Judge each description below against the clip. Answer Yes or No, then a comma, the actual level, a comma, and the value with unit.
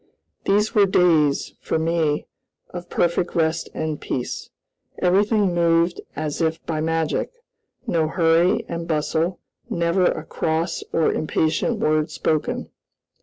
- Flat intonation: Yes, narrow, 1.9 semitones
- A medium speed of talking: No, slow, 125 wpm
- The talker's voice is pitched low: No, medium, 165 Hz